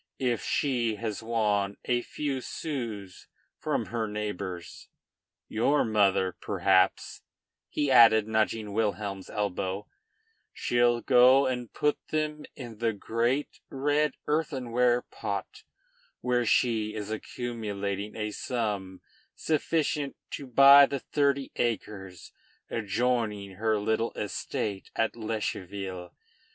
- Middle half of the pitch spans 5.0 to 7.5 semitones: No, average, 3.5 semitones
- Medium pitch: No, low, 115 Hz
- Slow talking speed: Yes, slow, 105 wpm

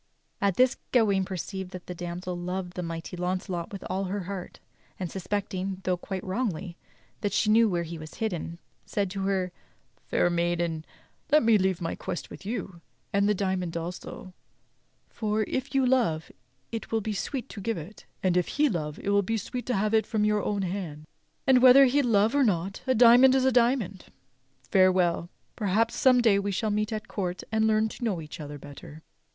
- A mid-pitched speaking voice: No, high, 195 Hz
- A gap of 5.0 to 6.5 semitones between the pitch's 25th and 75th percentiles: No, average, 3.8 semitones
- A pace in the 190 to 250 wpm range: Yes, average, 195 wpm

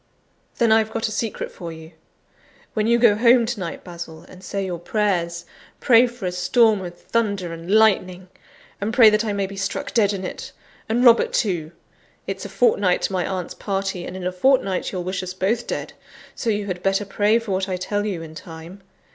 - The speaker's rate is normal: No, fast, 210 wpm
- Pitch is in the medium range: No, high, 195 Hz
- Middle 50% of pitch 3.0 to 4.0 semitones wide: Yes, average, 3.3 semitones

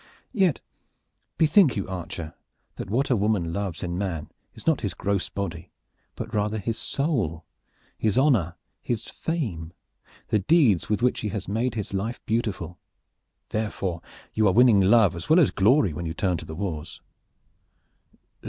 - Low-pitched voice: Yes, low, 100 Hz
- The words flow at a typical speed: Yes, average, 160 wpm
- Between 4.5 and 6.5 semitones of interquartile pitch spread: Yes, average, 5.2 semitones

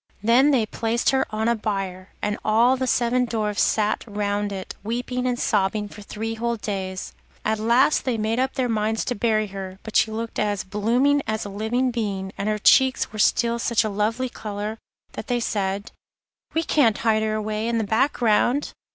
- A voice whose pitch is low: No, high, 220 Hz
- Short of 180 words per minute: No, average, 195 wpm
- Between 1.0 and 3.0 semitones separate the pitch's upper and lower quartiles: Yes, narrow, 2.4 semitones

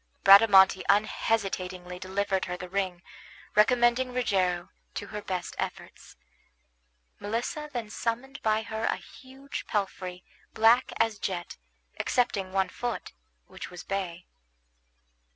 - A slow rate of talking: Yes, slow, 115 wpm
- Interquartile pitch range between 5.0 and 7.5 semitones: No, average, 3.7 semitones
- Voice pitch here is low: No, high, 205 Hz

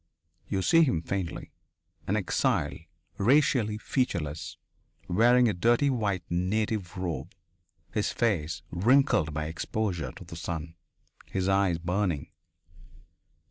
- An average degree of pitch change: Yes, average, 4.6 semitones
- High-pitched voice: No, very low, 95 Hz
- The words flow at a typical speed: No, slow, 110 wpm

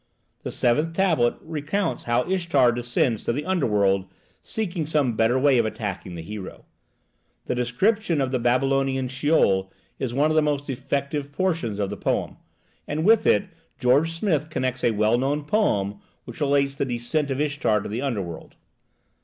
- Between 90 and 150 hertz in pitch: Yes, low, 135 Hz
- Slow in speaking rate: No, average, 165 wpm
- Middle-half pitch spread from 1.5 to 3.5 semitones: No, average, 4.5 semitones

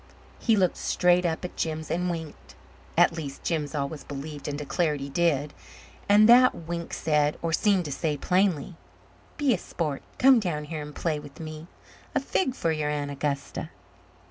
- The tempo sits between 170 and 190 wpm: Yes, average, 175 wpm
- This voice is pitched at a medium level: Yes, medium, 160 Hz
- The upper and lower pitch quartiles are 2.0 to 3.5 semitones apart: Yes, average, 3.2 semitones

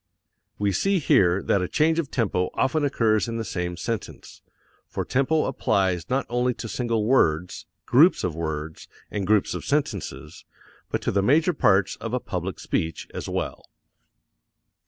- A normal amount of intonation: No, wide, 6.5 semitones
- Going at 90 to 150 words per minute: No, average, 160 wpm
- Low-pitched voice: Yes, low, 110 Hz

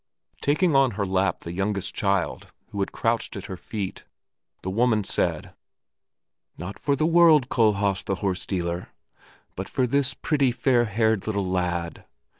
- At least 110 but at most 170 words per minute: Yes, average, 155 wpm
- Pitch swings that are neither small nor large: Yes, average, 4.9 semitones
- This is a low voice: Yes, low, 105 Hz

